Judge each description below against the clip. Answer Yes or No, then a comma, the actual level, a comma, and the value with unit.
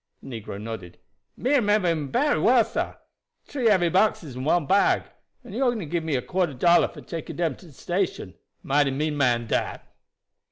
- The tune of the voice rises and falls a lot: Yes, wide, 6.8 semitones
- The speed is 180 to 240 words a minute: Yes, average, 185 wpm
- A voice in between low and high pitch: Yes, medium, 165 Hz